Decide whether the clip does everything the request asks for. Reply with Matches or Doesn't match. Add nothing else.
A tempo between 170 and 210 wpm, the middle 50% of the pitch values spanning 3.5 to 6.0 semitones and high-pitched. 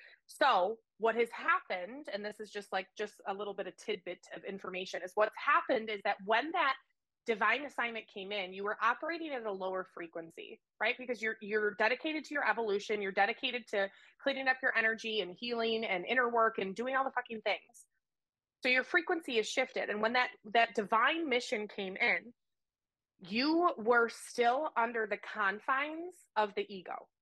Matches